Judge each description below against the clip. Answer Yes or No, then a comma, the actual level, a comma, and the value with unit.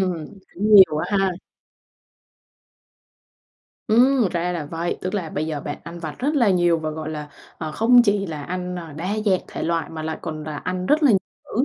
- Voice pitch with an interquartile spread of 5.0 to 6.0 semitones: No, average, 4.3 semitones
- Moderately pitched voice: Yes, medium, 175 Hz